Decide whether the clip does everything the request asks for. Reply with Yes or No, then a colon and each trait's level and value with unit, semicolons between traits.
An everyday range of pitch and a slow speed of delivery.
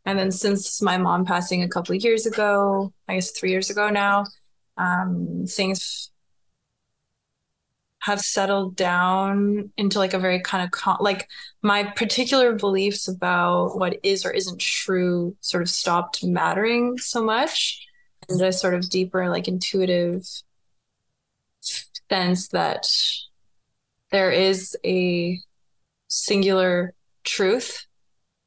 No: narrow, 2.2 semitones; slow, 125 wpm